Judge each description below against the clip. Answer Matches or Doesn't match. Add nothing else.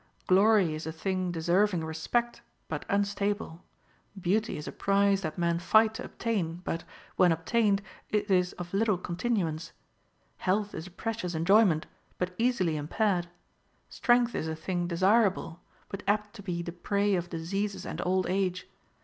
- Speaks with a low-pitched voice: Doesn't match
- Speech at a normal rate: Matches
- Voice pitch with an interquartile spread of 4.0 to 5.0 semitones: Doesn't match